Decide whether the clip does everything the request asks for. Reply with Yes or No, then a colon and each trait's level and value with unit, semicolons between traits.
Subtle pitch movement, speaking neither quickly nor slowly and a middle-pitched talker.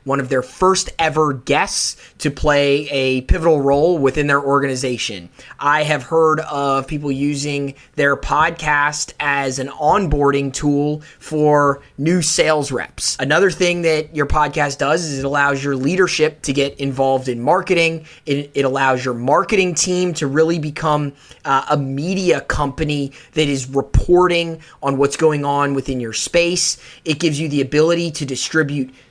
Yes: narrow, 2.3 semitones; average, 155 wpm; medium, 145 Hz